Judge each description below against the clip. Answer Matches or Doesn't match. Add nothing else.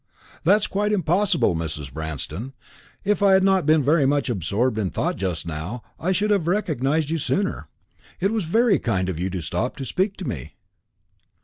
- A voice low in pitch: Doesn't match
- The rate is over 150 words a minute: Matches